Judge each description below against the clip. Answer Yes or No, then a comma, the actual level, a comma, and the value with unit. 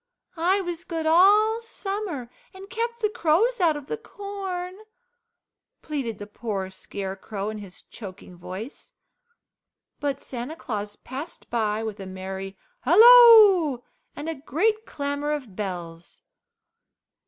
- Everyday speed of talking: No, slow, 125 wpm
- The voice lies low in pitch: No, very high, 290 Hz